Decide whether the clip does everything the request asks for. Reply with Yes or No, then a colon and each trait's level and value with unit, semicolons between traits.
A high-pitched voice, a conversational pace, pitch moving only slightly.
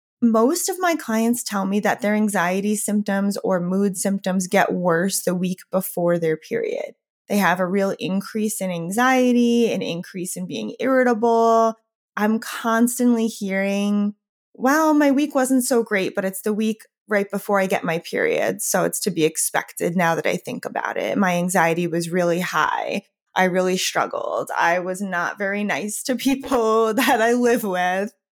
No: high, 205 Hz; average, 170 wpm; average, 3.8 semitones